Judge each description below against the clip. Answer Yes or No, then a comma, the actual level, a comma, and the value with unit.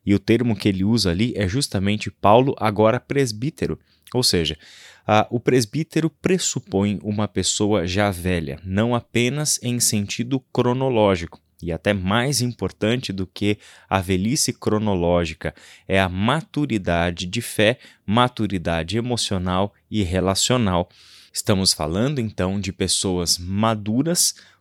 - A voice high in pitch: No, low, 105 Hz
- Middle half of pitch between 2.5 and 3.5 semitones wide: No, average, 4.4 semitones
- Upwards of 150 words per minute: No, average, 125 wpm